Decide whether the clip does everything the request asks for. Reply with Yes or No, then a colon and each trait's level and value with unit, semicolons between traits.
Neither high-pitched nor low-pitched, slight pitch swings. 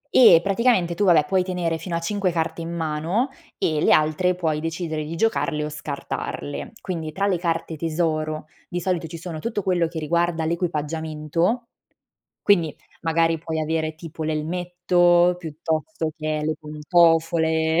Yes: medium, 165 Hz; narrow, 2.1 semitones